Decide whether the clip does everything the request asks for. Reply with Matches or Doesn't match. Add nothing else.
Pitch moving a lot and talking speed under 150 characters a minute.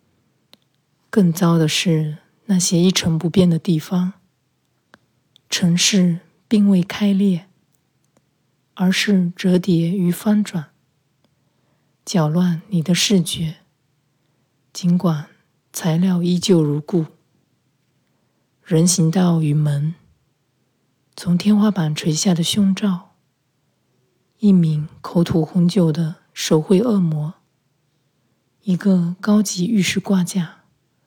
Doesn't match